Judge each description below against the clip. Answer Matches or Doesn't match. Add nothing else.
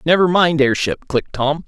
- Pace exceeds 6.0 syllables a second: Doesn't match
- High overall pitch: Doesn't match